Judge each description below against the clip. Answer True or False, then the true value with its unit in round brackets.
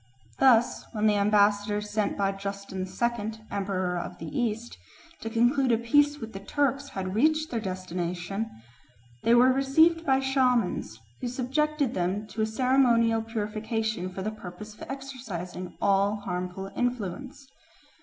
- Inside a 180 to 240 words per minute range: False (145 wpm)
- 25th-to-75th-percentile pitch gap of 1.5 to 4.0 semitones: False (4.5 semitones)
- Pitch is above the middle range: True (220 Hz)